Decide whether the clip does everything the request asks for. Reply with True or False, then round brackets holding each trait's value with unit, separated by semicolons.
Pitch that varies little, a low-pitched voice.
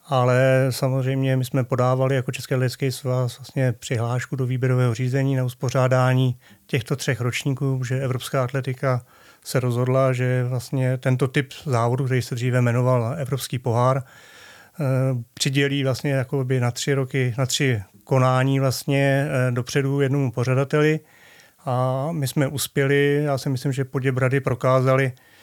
True (1.4 semitones; 130 Hz)